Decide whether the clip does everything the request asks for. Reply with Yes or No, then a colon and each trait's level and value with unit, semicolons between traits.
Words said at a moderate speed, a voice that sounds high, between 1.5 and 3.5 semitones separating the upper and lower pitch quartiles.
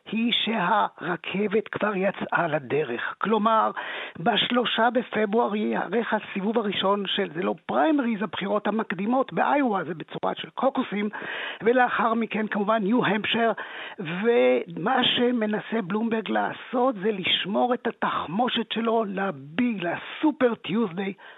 Yes: average, 110 wpm; high, 220 Hz; average, 2.9 semitones